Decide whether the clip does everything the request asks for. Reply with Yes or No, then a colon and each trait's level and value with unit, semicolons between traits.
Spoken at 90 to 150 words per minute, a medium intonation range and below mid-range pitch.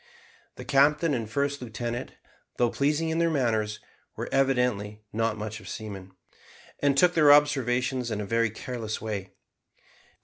Yes: average, 145 wpm; average, 4.7 semitones; low, 120 Hz